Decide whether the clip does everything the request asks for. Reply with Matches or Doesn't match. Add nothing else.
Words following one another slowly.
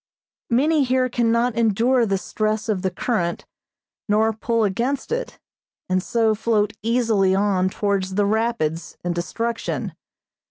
Matches